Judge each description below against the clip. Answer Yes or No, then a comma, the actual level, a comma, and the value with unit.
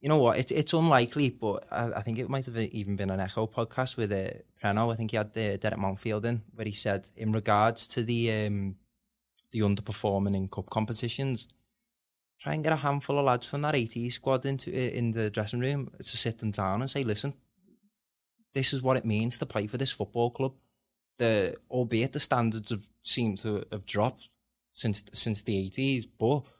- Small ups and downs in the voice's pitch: No, average, 3.6 semitones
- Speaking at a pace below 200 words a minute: No, fast, 205 wpm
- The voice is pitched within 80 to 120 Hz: Yes, low, 115 Hz